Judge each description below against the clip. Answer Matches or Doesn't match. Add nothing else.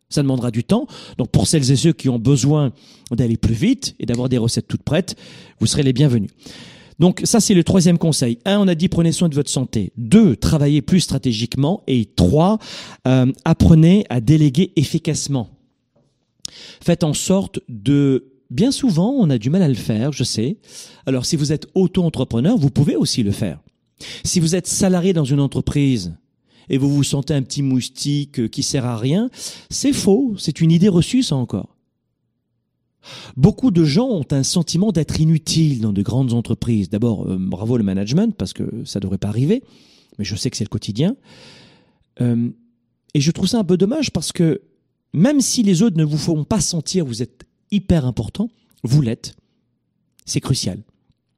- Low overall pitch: Doesn't match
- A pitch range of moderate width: Doesn't match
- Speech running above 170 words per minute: Matches